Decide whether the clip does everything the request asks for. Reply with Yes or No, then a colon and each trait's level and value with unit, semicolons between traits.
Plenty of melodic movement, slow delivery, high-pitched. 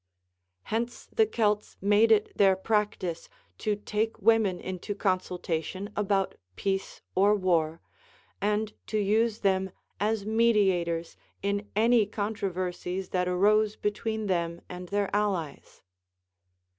No: narrow, 2.5 semitones; slow, 115 wpm; high, 205 Hz